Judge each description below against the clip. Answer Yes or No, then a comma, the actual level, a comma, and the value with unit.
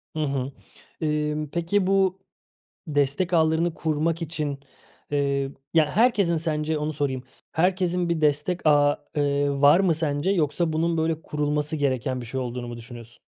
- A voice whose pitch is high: No, medium, 150 Hz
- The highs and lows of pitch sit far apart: No, average, 2.9 semitones